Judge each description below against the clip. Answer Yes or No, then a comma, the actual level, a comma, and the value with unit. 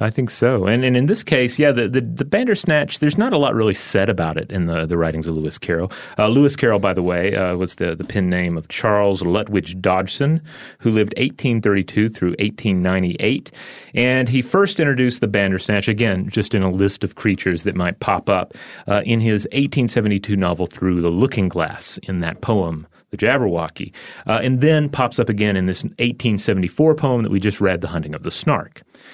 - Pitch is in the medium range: No, low, 105 Hz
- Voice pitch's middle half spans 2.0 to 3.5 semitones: No, wide, 5.4 semitones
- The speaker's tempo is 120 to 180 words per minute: No, fast, 205 wpm